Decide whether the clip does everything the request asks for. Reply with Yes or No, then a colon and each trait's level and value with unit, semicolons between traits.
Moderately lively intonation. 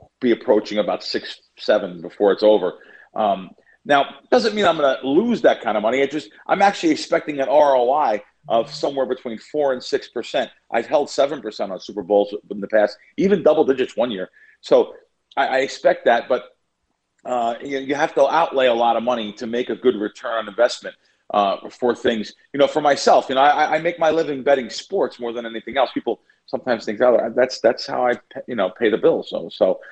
No: wide, 6.1 semitones